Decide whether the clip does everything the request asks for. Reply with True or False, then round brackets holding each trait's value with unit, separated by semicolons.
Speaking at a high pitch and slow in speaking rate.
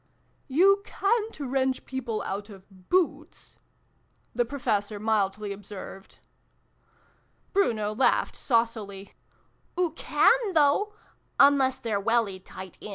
True (235 Hz; 105 wpm)